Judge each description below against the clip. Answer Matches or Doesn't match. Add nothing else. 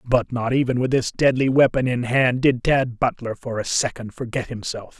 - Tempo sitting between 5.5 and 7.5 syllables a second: Doesn't match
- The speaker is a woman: Doesn't match